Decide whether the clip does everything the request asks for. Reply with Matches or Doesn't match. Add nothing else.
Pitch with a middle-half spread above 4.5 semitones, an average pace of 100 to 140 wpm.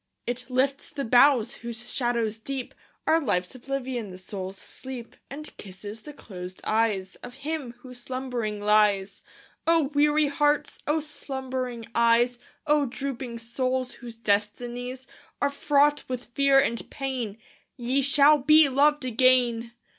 Doesn't match